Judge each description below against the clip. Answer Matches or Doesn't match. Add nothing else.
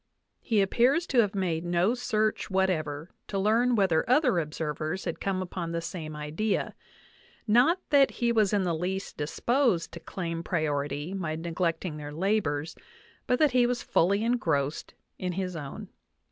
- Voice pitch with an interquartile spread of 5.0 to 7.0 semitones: Matches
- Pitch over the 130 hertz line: Matches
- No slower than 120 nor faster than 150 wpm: Doesn't match